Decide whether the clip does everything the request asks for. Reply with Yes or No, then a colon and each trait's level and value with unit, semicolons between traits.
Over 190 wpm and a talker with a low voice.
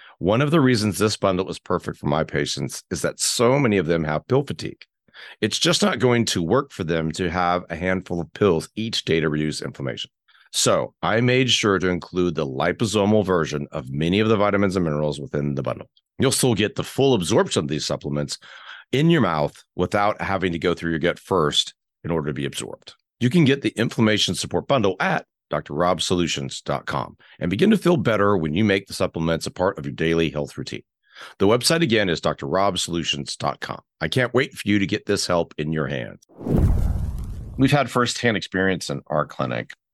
Yes: average, 200 wpm; very low, 90 Hz